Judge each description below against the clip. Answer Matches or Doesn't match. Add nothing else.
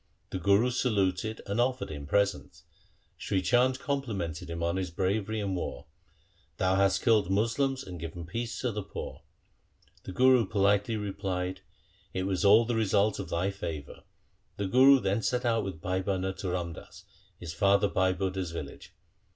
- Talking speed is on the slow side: Doesn't match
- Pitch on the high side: Doesn't match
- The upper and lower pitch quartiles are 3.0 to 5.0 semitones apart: Matches